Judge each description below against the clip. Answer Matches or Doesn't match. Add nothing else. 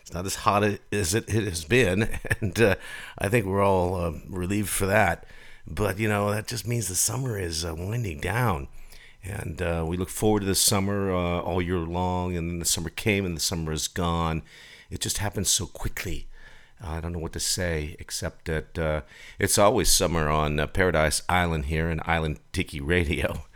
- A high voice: Doesn't match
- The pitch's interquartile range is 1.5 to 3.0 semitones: Doesn't match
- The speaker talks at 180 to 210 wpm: Matches